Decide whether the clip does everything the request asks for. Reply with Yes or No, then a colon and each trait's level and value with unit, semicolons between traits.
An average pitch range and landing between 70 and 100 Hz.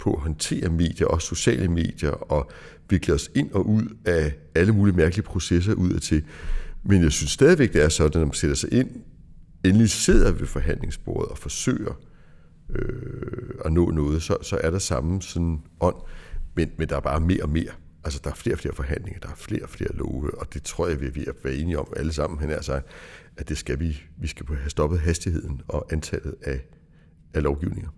Yes: average, 3.4 semitones; very low, 80 Hz